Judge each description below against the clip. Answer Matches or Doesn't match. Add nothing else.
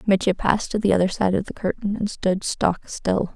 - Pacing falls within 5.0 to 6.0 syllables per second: Matches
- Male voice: Doesn't match